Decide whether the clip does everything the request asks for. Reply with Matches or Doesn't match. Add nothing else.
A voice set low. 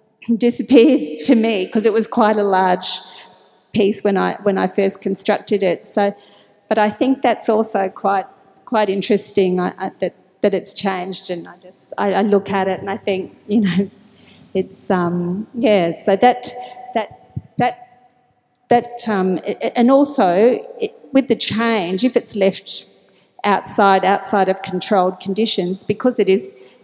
Doesn't match